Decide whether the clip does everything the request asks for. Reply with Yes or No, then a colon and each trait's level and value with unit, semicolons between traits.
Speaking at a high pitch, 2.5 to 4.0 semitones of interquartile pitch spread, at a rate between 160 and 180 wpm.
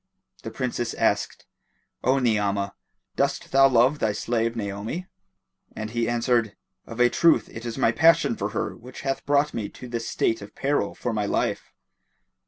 No: low, 115 Hz; average, 2.8 semitones; average, 170 wpm